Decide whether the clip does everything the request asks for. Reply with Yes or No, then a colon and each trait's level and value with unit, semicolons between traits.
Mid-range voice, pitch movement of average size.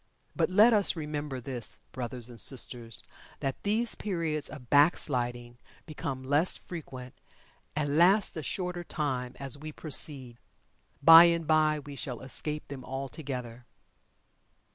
Yes: medium, 145 Hz; average, 4.2 semitones